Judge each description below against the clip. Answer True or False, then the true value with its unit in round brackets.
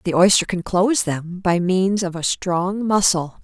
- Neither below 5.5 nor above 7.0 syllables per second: False (4.3 syllables/s)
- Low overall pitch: False (185 Hz)